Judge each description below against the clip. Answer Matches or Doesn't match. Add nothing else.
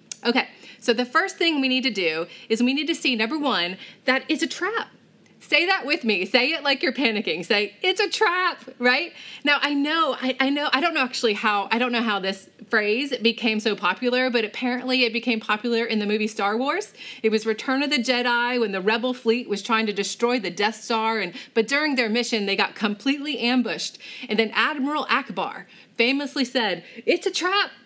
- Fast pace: Matches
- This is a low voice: Doesn't match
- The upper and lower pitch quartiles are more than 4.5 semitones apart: Doesn't match